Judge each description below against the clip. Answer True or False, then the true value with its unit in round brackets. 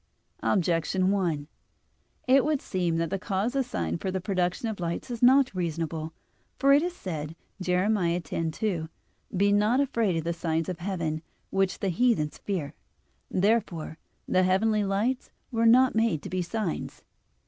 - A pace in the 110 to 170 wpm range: True (160 wpm)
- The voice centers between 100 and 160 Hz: False (185 Hz)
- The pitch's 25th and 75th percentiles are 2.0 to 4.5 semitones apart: False (5.0 semitones)